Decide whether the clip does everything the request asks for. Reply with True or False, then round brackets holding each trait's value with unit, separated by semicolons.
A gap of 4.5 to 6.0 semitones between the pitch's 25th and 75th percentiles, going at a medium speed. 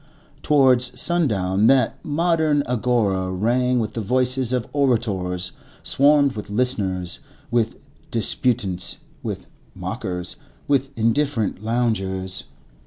False (5.1 semitones; 100 wpm)